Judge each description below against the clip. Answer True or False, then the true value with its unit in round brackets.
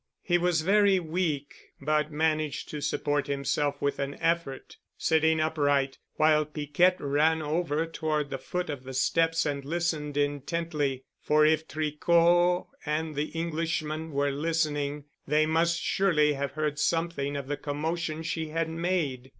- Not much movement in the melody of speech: True (2.3 semitones)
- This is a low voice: False (155 Hz)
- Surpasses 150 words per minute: False (145 wpm)